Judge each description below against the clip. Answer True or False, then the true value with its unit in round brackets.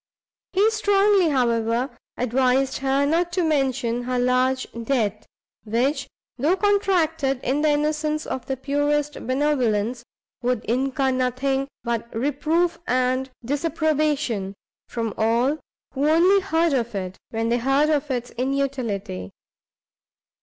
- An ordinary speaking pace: False (120 wpm)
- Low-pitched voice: False (270 Hz)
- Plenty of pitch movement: False (3.9 semitones)